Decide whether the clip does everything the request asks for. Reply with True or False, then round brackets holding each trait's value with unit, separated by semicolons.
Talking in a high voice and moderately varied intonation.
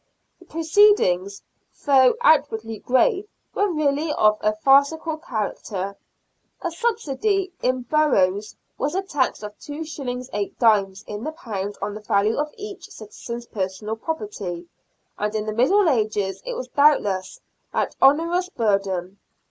False (255 Hz; 7.4 semitones)